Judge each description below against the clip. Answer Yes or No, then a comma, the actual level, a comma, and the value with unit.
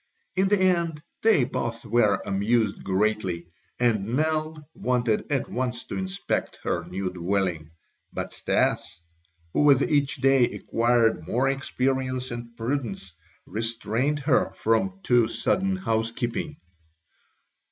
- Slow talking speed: Yes, slow, 120 wpm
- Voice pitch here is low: Yes, low, 120 Hz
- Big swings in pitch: No, average, 4.9 semitones